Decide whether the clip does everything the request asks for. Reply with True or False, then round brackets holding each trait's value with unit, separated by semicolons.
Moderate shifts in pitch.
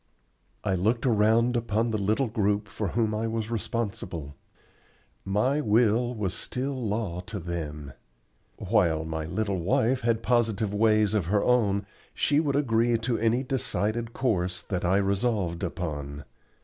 True (3.7 semitones)